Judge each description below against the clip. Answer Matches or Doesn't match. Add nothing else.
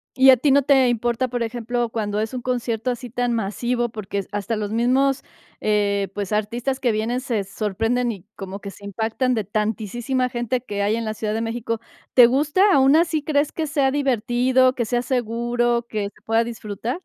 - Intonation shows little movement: Doesn't match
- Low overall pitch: Doesn't match